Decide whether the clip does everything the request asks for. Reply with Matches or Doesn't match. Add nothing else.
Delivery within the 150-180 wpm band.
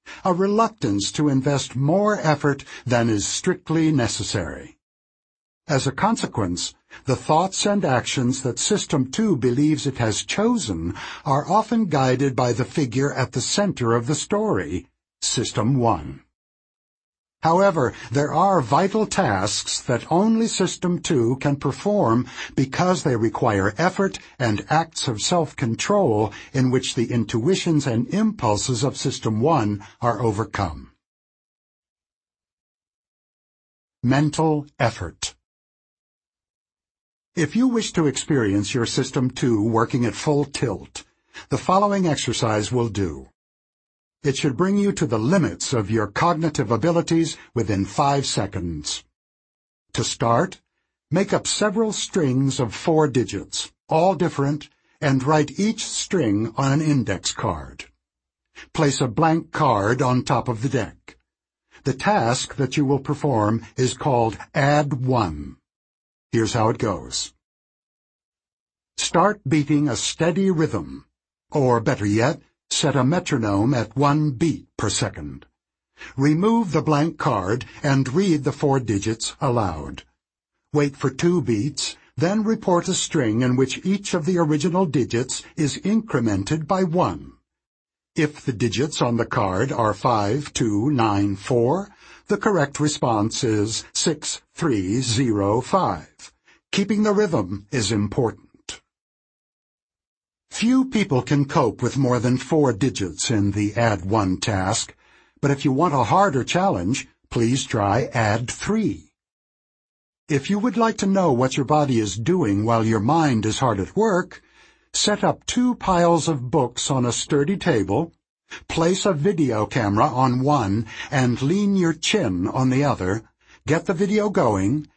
Doesn't match